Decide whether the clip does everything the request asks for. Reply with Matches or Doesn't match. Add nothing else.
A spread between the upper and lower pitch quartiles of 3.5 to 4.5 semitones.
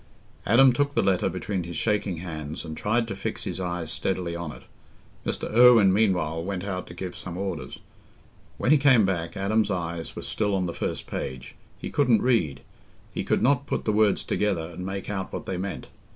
Matches